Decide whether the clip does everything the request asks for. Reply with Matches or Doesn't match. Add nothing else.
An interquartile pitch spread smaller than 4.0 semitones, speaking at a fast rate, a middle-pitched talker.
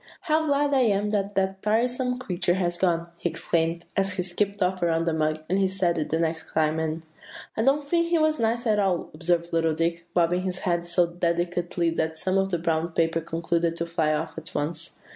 Matches